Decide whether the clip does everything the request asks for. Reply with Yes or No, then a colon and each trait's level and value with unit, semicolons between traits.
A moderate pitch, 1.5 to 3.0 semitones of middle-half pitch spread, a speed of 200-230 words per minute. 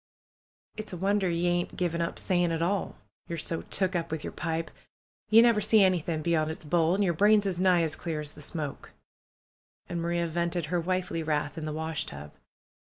Yes: medium, 170 Hz; narrow, 2.5 semitones; fast, 205 wpm